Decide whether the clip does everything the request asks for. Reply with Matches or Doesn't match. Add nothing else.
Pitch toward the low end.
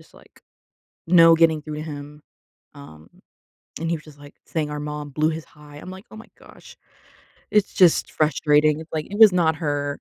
Doesn't match